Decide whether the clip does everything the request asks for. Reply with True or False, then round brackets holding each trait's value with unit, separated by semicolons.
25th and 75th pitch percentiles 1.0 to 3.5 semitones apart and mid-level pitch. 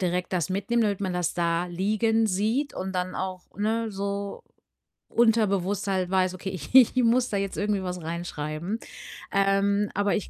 False (2.6 semitones; 195 Hz)